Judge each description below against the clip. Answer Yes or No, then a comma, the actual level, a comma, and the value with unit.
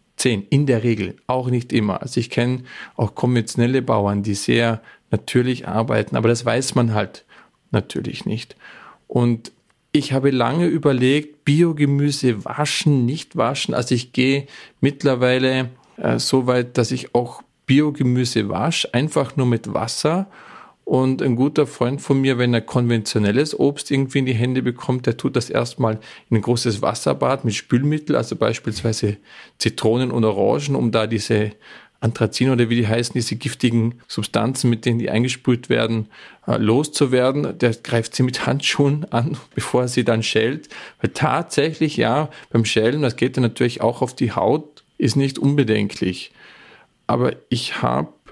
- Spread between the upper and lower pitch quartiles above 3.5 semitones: No, average, 3.1 semitones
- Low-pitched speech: Yes, low, 125 Hz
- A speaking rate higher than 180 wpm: No, average, 155 wpm